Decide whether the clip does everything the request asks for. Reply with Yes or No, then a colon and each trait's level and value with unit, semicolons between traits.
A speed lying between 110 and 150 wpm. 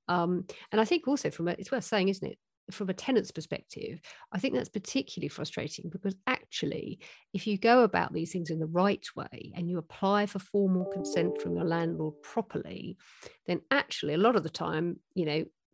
No: average, 200 wpm